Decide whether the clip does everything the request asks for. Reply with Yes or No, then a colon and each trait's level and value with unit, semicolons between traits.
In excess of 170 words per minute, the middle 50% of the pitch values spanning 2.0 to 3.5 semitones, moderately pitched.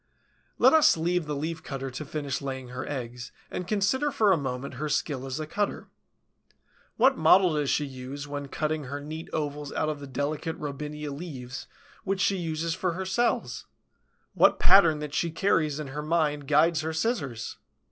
Yes: average, 180 wpm; average, 3.2 semitones; medium, 150 Hz